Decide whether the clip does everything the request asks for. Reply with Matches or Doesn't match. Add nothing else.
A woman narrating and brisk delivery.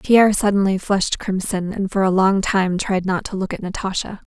Matches